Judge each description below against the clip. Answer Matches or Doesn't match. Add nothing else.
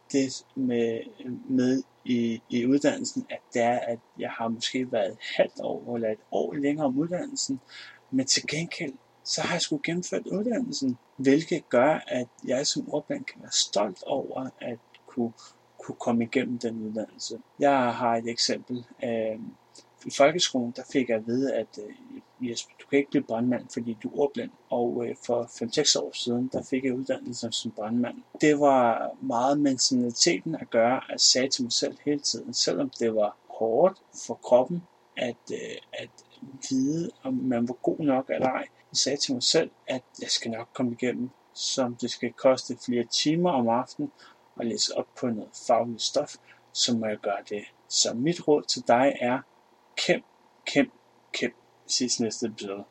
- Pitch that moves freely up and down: Doesn't match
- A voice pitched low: Matches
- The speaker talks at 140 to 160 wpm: Doesn't match